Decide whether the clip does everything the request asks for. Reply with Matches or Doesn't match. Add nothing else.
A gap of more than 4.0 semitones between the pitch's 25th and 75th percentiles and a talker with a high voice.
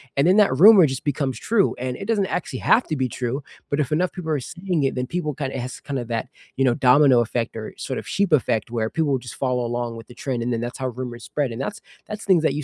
Doesn't match